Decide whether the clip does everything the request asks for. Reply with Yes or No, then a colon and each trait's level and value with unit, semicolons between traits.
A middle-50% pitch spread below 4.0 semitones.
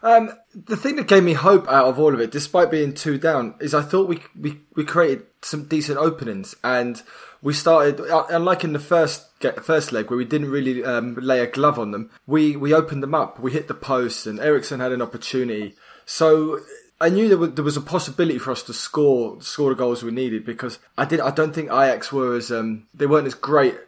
No: average, 4.4 semitones